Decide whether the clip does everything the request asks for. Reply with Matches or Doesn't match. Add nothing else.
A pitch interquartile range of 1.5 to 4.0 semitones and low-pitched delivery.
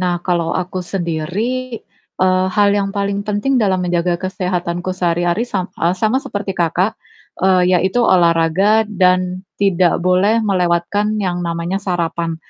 Doesn't match